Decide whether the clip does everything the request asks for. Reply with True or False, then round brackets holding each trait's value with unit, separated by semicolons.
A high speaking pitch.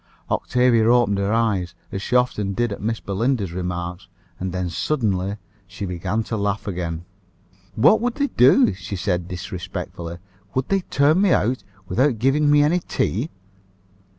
False (105 Hz)